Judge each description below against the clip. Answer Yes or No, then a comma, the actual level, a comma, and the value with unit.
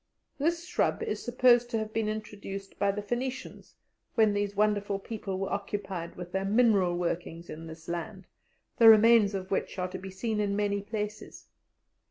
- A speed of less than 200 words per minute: Yes, average, 175 wpm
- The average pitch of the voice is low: No, high, 205 Hz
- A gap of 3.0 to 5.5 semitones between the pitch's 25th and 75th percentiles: No, narrow, 2.6 semitones